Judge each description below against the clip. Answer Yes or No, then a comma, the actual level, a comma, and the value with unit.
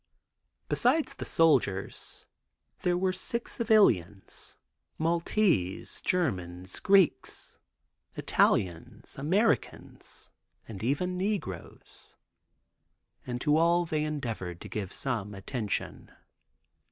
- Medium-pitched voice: Yes, medium, 145 Hz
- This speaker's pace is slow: Yes, slow, 85 wpm